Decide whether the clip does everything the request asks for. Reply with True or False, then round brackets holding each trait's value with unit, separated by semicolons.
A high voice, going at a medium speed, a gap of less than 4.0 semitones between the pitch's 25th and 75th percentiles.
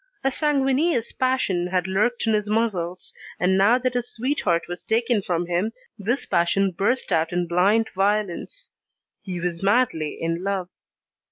False (200 Hz; 155 wpm; 5.4 semitones)